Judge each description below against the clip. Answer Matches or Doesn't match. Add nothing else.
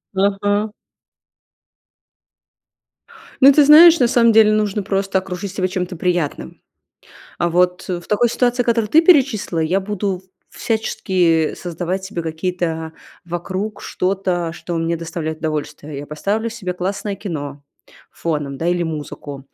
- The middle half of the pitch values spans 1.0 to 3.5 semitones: Doesn't match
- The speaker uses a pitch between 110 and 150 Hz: Doesn't match